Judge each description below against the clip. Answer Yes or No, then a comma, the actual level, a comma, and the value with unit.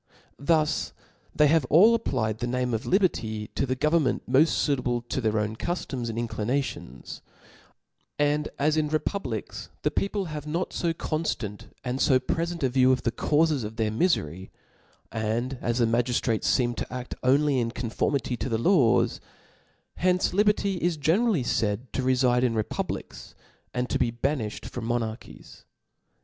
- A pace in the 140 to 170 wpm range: Yes, average, 160 wpm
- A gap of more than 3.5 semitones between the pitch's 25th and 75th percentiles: Yes, average, 4.8 semitones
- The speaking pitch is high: No, low, 130 Hz